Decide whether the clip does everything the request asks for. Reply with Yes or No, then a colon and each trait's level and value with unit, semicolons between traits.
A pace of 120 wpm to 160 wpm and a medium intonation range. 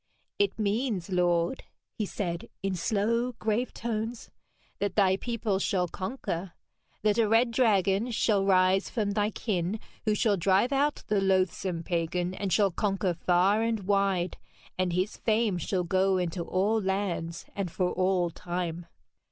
Yes: average, 150 wpm; average, 3.1 semitones